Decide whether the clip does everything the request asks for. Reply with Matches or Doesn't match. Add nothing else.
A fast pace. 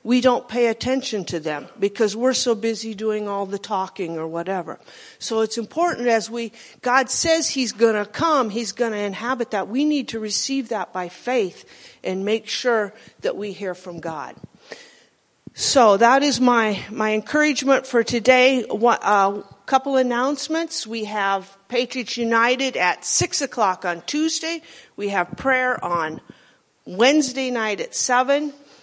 Doesn't match